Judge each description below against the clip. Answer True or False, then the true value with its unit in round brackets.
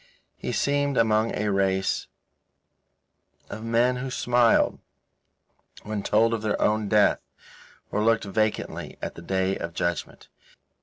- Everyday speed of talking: False (130 wpm)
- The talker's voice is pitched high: False (110 Hz)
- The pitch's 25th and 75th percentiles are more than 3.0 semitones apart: False (2.7 semitones)